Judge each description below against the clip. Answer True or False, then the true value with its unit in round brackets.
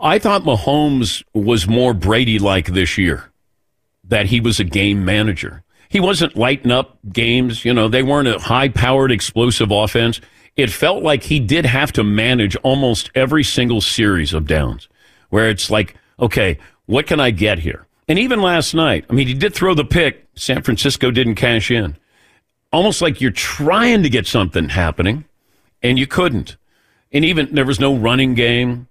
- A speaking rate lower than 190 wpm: True (180 wpm)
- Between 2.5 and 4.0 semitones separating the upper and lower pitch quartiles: False (4.4 semitones)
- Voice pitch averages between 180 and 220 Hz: False (120 Hz)